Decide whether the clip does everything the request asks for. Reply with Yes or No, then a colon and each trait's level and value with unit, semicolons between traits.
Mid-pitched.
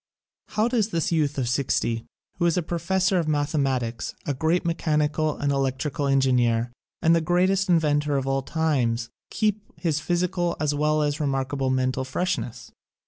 Yes: medium, 150 Hz